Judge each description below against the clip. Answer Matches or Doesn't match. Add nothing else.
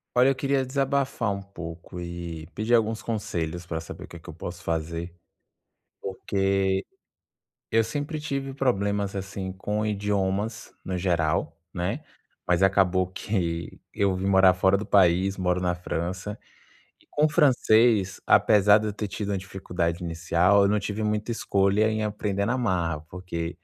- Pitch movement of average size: Matches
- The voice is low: Matches